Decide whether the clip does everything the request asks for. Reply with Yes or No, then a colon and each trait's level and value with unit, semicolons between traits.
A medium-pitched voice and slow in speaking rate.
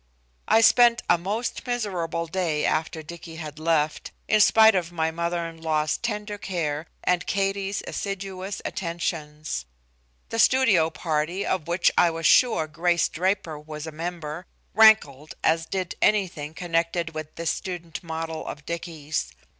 No: medium, 170 Hz; average, 145 wpm